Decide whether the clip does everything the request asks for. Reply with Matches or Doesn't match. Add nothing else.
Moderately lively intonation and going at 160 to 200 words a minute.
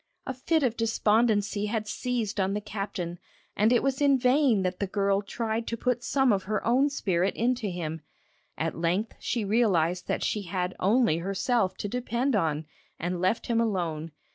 Matches